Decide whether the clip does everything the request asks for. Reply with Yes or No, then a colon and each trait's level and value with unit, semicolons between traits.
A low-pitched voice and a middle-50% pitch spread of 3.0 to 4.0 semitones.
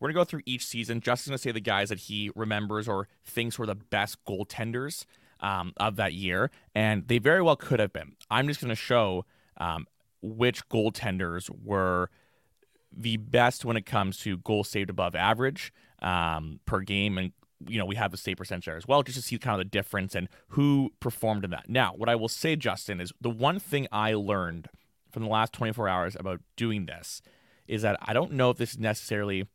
Yes: low, 110 Hz; average, 3.6 semitones